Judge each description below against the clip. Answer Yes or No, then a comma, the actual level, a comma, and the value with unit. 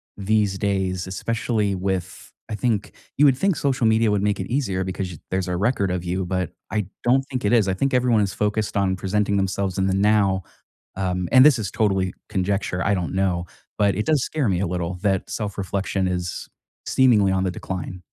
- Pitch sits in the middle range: No, low, 100 Hz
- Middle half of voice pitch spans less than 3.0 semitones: Yes, narrow, 2.5 semitones